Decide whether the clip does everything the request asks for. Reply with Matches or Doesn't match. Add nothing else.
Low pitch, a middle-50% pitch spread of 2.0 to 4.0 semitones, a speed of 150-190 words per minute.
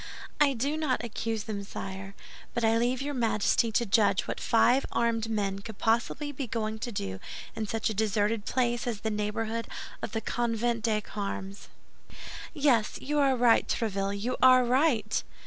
Doesn't match